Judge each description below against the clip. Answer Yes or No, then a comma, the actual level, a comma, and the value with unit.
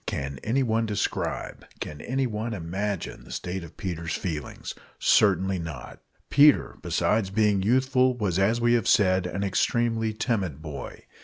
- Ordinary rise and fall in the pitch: Yes, average, 4.6 semitones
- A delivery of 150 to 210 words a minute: No, average, 140 wpm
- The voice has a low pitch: Yes, low, 100 Hz